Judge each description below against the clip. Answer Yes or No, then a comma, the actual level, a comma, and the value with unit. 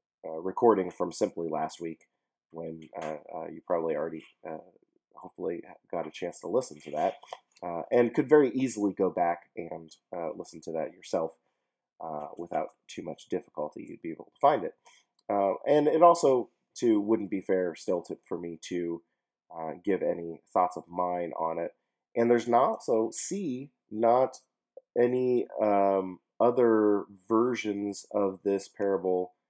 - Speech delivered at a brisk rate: No, average, 160 wpm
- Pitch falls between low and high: No, low, 100 Hz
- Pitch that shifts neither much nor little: No, wide, 5.7 semitones